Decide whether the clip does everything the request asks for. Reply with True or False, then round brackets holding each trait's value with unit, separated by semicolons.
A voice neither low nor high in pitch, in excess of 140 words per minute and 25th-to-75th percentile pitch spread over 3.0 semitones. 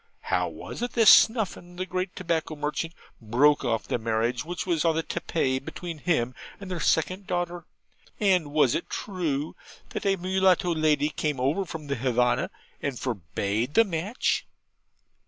True (160 Hz; 160 wpm; 5.6 semitones)